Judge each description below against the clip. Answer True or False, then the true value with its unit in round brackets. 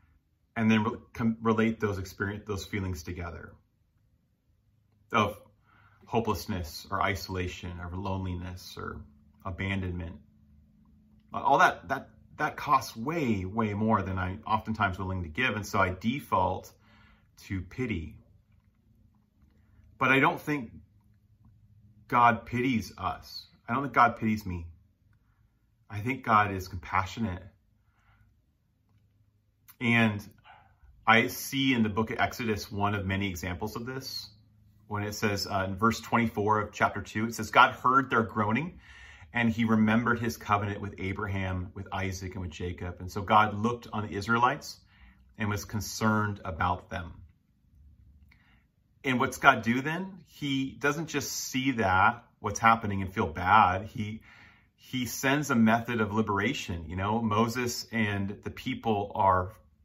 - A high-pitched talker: False (105 Hz)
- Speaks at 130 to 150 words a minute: True (140 wpm)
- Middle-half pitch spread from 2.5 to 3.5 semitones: True (2.8 semitones)